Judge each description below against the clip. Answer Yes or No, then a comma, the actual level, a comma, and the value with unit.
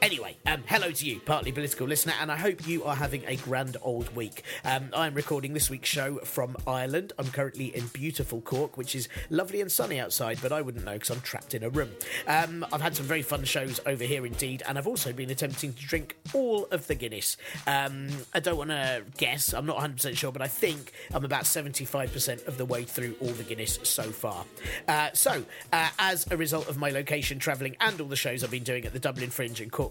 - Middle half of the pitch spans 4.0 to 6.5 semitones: No, average, 3.0 semitones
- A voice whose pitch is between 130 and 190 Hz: Yes, medium, 140 Hz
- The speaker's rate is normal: No, fast, 235 wpm